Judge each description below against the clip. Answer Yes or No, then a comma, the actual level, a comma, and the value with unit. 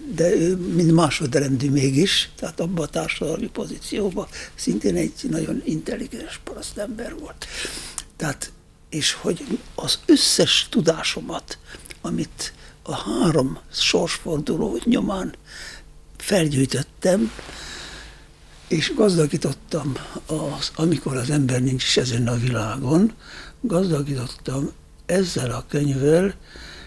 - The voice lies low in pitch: No, medium, 150 Hz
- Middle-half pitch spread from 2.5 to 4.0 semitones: No, average, 4.8 semitones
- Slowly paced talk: Yes, slow, 100 wpm